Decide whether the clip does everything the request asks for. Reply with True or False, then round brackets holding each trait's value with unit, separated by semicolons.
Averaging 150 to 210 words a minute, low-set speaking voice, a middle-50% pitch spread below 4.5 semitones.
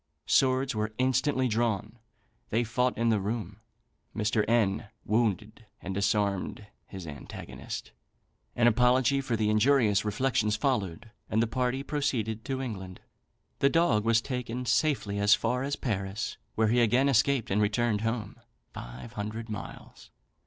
False (140 wpm; 115 Hz; 3.2 semitones)